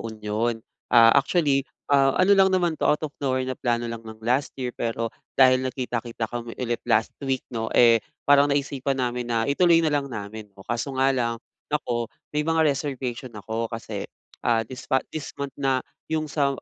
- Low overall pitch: Yes, low, 130 Hz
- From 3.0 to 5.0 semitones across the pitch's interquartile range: Yes, average, 3.3 semitones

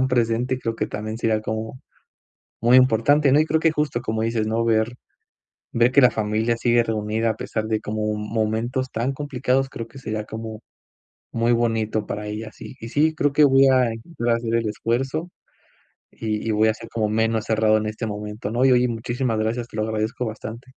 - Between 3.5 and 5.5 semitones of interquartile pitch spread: No, narrow, 2.4 semitones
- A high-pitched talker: No, low, 115 Hz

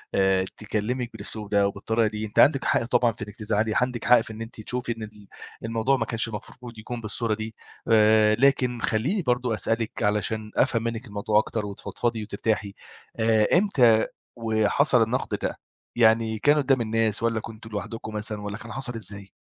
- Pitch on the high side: No, low, 110 Hz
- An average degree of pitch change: No, narrow, 1.8 semitones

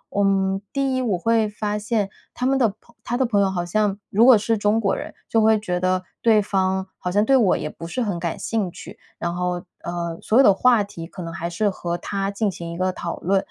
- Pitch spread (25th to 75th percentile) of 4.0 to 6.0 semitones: No, average, 3.6 semitones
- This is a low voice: No, high, 200 Hz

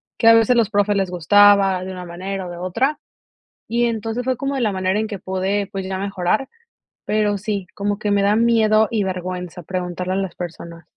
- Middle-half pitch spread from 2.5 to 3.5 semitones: Yes, average, 2.8 semitones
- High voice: Yes, high, 200 Hz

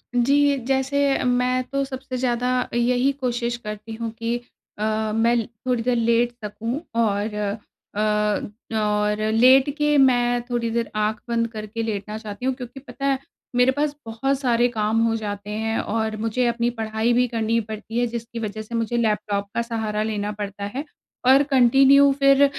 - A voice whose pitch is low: No, high, 235 Hz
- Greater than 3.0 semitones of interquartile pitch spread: No, average, 2.7 semitones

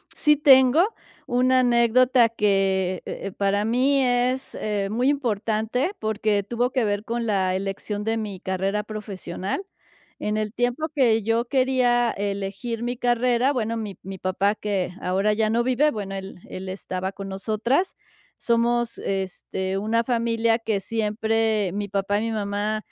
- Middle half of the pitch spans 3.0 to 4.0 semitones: Yes, average, 3.3 semitones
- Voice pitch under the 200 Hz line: No, high, 220 Hz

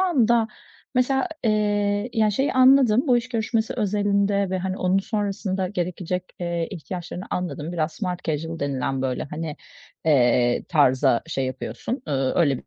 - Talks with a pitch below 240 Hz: Yes, medium, 185 Hz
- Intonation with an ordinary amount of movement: No, wide, 5.7 semitones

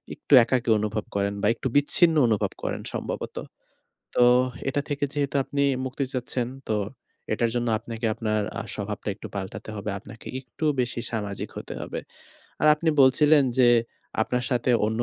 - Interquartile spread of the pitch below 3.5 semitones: No, average, 4.1 semitones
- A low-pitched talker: Yes, low, 120 Hz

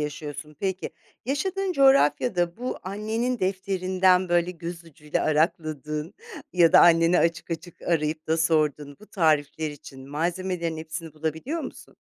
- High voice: No, medium, 170 Hz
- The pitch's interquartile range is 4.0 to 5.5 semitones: No, average, 3.3 semitones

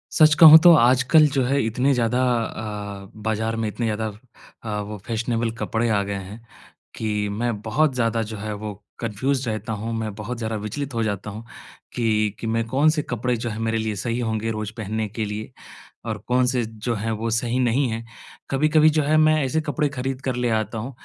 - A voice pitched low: Yes, low, 115 Hz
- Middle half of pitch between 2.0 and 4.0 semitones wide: Yes, average, 2.9 semitones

